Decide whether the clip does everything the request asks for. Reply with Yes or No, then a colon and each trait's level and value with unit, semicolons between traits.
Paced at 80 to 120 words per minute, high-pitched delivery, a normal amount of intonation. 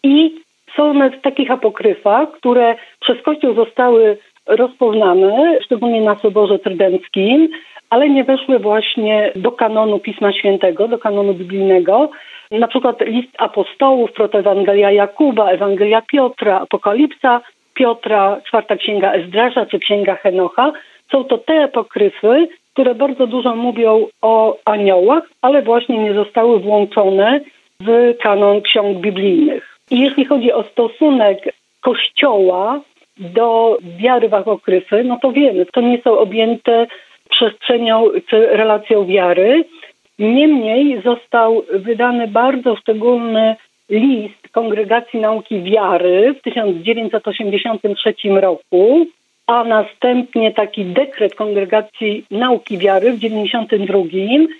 Yes: slow, 110 wpm; high, 225 Hz; average, 3.7 semitones